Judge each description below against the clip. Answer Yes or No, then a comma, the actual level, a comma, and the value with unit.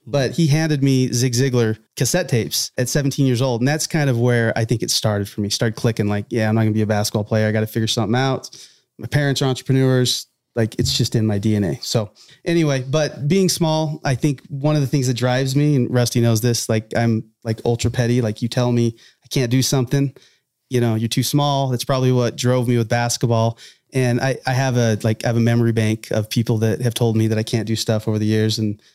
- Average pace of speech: No, fast, 250 wpm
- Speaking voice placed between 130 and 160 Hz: No, low, 120 Hz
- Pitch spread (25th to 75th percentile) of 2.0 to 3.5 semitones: Yes, average, 2.9 semitones